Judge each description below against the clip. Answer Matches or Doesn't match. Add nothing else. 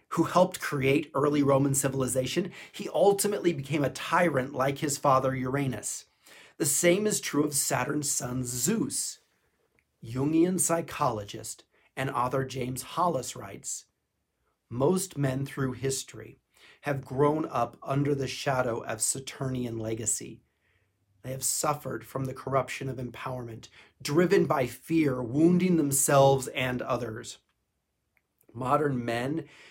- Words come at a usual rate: Doesn't match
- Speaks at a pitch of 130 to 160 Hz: Matches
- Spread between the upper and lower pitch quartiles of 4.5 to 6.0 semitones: Doesn't match